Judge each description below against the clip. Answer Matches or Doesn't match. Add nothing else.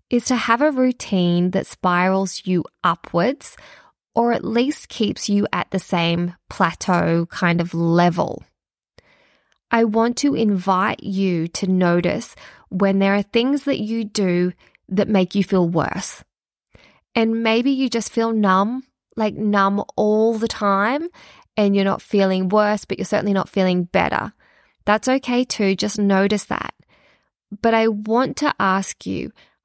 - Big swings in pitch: Doesn't match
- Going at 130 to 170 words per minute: Matches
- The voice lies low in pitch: Doesn't match